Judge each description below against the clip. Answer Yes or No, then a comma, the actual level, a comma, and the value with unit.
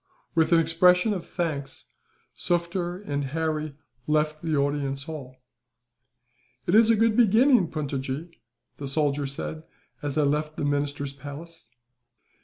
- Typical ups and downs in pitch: Yes, average, 3.4 semitones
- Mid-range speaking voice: Yes, medium, 155 Hz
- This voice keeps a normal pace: No, slow, 130 wpm